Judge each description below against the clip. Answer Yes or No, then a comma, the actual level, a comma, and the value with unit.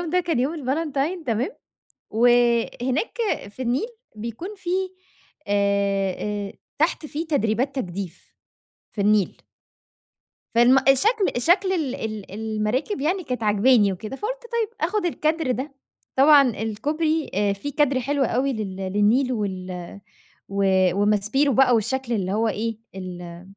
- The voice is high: Yes, high, 245 Hz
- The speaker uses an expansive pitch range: Yes, wide, 6.2 semitones